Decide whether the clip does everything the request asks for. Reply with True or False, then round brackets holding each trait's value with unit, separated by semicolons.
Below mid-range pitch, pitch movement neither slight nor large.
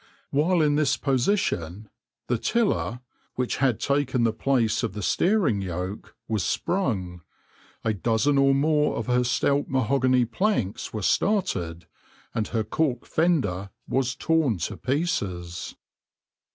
False (125 Hz; 5.8 semitones)